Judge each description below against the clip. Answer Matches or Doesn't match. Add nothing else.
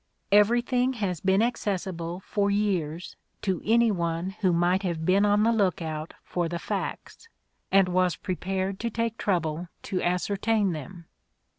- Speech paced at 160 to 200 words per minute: Doesn't match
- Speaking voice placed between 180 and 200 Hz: Matches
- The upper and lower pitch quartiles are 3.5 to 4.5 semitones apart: Doesn't match